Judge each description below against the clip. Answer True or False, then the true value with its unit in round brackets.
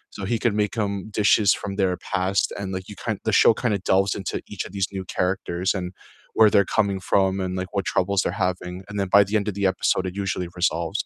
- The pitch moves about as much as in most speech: False (1.6 semitones)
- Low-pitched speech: True (95 Hz)